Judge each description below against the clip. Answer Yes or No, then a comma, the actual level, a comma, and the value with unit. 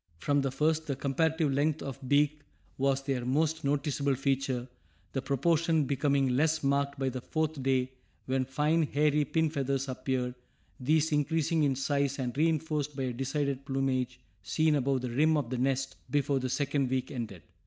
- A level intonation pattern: Yes, narrow, 2.3 semitones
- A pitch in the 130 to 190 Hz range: Yes, medium, 140 Hz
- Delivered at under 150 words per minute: No, average, 170 wpm